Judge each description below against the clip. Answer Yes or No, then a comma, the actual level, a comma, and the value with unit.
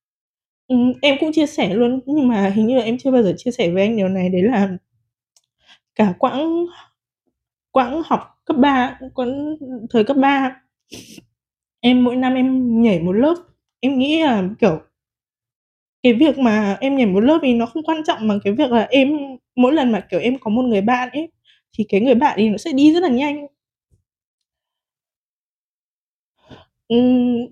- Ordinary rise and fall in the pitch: Yes, average, 4.3 semitones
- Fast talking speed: No, average, 180 wpm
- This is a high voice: Yes, very high, 250 Hz